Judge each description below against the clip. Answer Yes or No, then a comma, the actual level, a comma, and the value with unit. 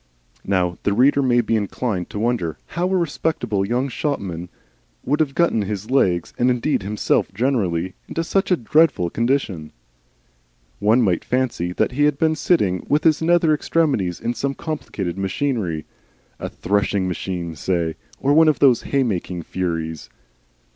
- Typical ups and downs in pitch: No, wide, 7.6 semitones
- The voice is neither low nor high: No, low, 115 Hz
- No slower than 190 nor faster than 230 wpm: No, average, 155 wpm